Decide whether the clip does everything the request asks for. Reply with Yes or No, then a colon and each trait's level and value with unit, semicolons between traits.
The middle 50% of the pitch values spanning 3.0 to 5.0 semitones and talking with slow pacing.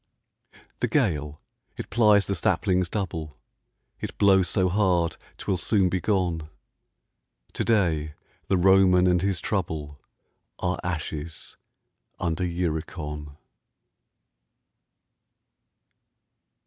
Yes: average, 3.3 semitones; slow, 95 wpm